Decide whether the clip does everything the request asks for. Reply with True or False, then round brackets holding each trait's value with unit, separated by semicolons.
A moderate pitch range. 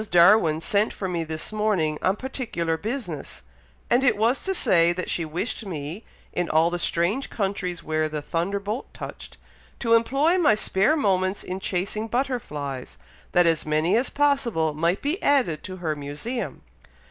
False (6.0 semitones)